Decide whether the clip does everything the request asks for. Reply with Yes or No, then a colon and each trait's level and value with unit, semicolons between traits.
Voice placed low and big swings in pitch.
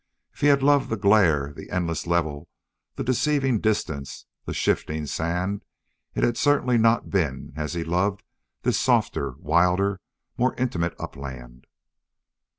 Yes: very low, 90 Hz; wide, 6.6 semitones